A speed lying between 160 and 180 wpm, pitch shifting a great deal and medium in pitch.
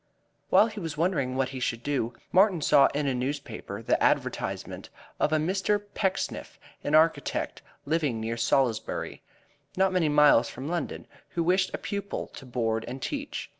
Yes: average, 165 wpm; wide, 6.2 semitones; medium, 150 Hz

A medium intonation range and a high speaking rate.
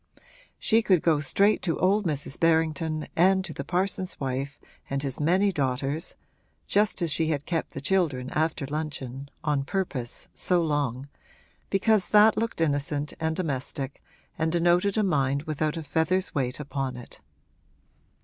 No: average, 4.6 semitones; average, 150 wpm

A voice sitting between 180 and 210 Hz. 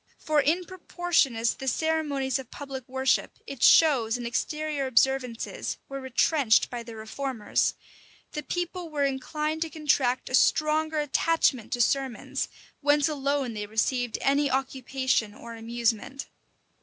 No: very high, 270 Hz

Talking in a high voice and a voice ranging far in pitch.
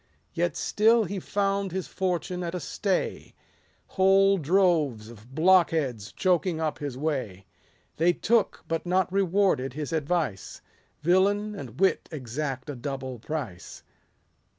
No: medium, 165 Hz; wide, 5.7 semitones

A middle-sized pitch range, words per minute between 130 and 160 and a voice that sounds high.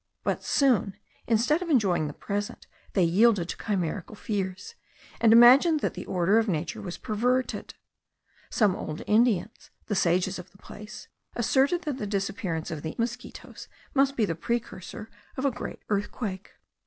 Yes: average, 4.6 semitones; average, 155 wpm; high, 210 Hz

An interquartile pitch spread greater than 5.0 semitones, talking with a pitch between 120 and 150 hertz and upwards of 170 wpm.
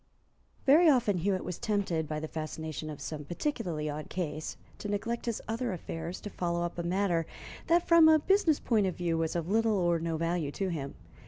No: wide, 5.5 semitones; medium, 175 Hz; average, 200 wpm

